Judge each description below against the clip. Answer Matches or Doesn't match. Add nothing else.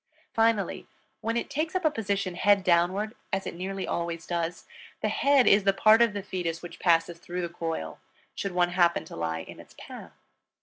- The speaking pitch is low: Doesn't match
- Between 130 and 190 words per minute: Doesn't match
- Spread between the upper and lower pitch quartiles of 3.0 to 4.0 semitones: Matches